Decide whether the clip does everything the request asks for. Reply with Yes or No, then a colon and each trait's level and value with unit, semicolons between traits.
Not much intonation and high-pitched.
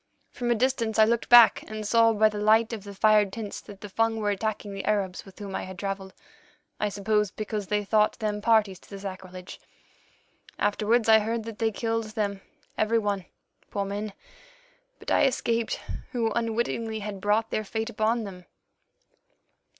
Yes: narrow, 2.0 semitones; high, 215 Hz